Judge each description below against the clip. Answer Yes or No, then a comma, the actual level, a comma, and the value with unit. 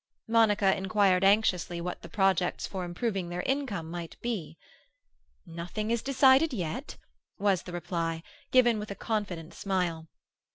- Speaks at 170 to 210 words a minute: No, slow, 135 wpm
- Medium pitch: No, high, 195 Hz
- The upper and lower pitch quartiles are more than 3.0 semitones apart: Yes, average, 4.1 semitones